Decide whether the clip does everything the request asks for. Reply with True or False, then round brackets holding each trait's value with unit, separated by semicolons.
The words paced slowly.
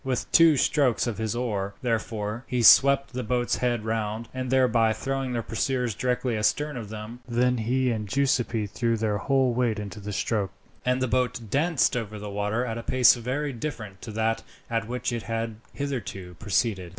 False (185 wpm)